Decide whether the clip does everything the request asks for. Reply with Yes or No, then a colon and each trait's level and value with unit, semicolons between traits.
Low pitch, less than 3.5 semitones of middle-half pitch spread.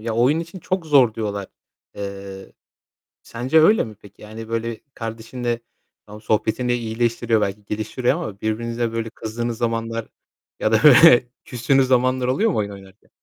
Yes: low, 115 Hz; narrow, 2.6 semitones